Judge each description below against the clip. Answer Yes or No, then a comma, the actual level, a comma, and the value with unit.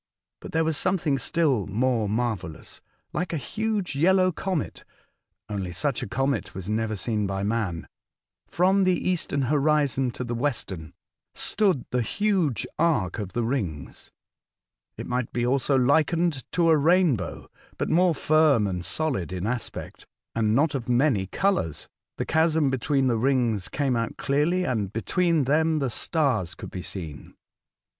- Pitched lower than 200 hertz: Yes, low, 135 Hz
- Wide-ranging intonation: Yes, wide, 6.7 semitones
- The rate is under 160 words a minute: Yes, average, 150 wpm